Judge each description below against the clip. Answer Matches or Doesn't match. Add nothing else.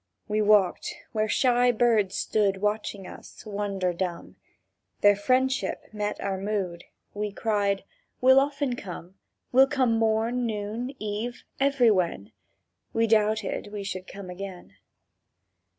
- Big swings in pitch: Doesn't match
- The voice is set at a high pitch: Matches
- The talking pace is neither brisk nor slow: Doesn't match